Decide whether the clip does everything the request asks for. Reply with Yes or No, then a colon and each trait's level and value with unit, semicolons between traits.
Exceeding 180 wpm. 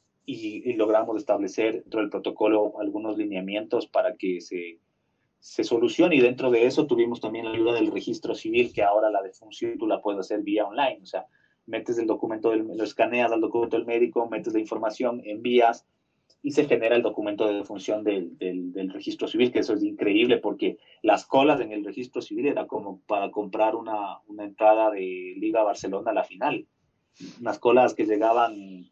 Yes: fast, 190 wpm